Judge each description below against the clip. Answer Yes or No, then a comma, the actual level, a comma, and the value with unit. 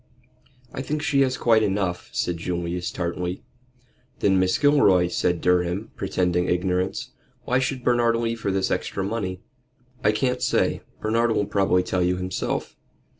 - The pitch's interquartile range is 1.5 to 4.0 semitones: No, average, 4.4 semitones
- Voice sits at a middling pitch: No, very low, 95 Hz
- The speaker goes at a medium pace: Yes, average, 150 wpm